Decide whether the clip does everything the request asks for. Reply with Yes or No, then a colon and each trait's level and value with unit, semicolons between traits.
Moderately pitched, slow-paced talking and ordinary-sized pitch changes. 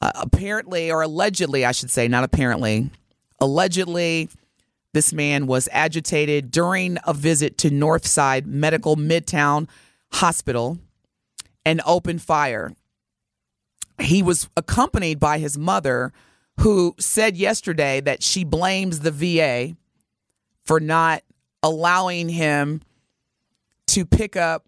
Yes: medium, 160 Hz; slow, 110 wpm; average, 3.2 semitones